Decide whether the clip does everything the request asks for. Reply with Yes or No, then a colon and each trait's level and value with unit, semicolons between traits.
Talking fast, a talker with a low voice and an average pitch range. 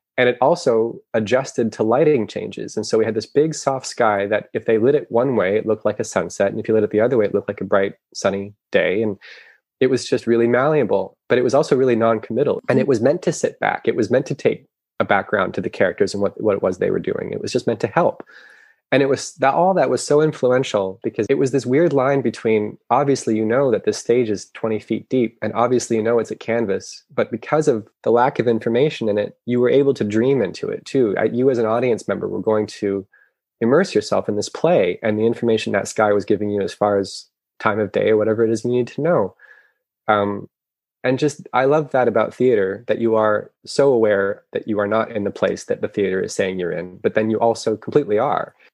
Yes: fast, 250 wpm; low, 115 Hz; average, 3.8 semitones